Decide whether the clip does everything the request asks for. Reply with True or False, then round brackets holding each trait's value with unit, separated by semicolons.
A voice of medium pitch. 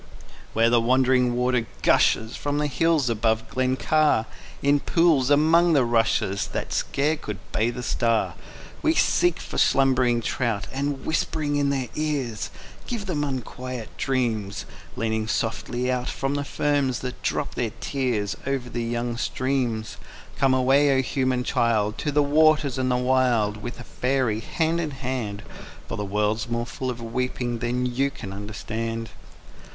False (125 Hz)